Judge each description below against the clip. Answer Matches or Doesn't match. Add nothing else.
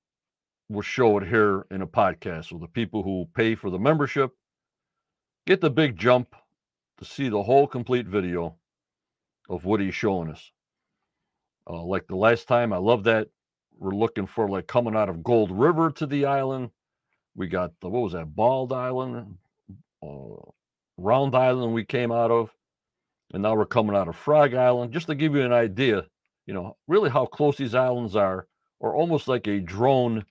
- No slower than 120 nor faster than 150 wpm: Doesn't match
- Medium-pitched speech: Doesn't match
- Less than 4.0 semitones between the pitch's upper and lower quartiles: Doesn't match